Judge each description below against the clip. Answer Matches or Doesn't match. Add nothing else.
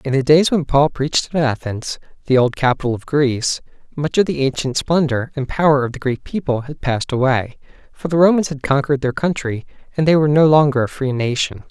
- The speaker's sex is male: Matches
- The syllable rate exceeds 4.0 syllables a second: Matches